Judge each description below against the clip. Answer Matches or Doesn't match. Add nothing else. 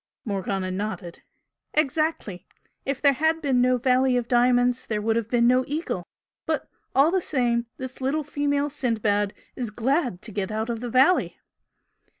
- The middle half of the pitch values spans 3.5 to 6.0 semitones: Matches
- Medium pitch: Doesn't match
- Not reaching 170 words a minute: Matches